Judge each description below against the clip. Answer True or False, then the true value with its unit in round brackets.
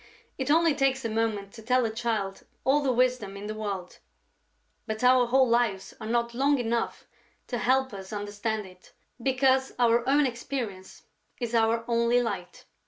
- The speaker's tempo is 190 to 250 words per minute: False (170 wpm)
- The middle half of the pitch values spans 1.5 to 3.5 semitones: True (3.0 semitones)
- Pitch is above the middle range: True (235 Hz)